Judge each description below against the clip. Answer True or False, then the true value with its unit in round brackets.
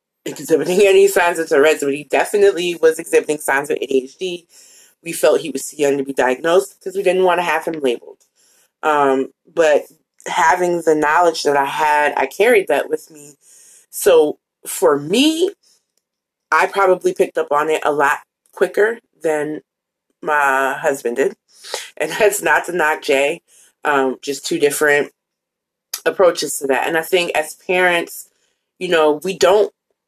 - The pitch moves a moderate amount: False (5.8 semitones)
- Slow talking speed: False (160 wpm)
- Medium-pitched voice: True (170 Hz)